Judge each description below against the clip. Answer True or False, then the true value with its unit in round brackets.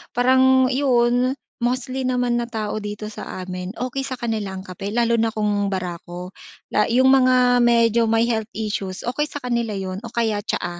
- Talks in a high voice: True (235 Hz)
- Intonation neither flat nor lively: True (3.3 semitones)